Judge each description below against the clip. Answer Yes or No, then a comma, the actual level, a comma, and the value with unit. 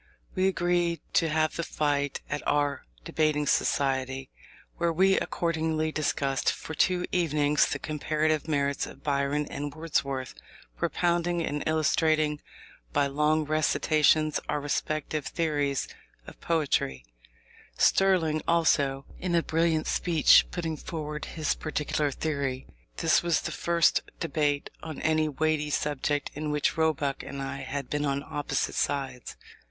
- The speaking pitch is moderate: Yes, medium, 150 Hz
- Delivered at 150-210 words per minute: No, slow, 135 wpm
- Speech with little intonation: Yes, narrow, 2.1 semitones